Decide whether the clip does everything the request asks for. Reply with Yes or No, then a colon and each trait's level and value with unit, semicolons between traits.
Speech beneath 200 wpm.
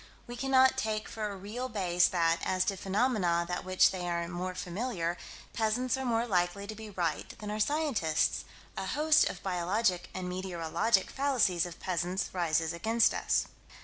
Yes: average, 170 wpm